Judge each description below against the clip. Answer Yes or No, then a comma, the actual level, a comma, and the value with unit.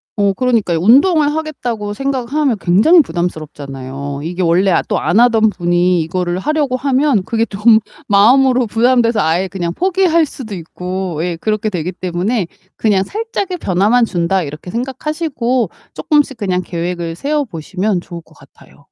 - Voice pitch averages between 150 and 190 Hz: No, high, 210 Hz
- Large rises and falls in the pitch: Yes, wide, 6.6 semitones